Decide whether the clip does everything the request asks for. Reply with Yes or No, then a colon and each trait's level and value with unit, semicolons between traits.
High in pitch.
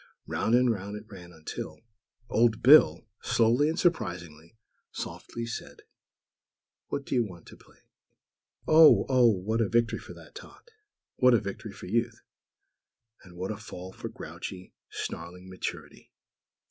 No: low, 110 Hz